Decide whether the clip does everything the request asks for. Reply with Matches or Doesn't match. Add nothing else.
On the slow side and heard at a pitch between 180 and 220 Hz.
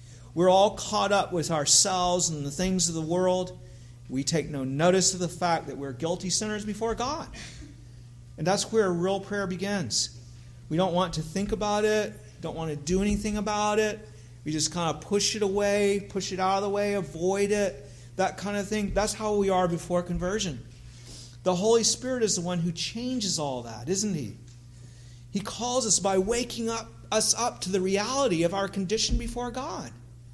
Doesn't match